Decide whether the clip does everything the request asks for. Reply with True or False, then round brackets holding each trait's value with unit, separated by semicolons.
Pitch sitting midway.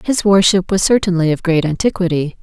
True (180 Hz)